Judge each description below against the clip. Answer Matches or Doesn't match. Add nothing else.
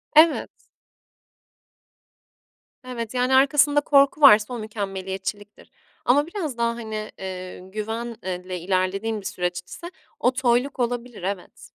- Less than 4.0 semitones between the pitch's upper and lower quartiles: Doesn't match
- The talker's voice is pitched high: Matches